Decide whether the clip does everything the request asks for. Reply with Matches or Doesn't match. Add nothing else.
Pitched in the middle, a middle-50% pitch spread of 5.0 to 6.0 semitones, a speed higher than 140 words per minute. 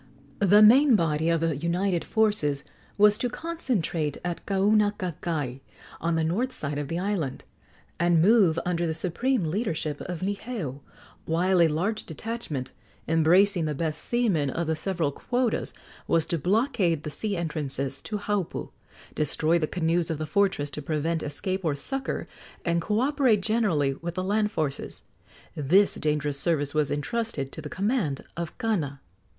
Matches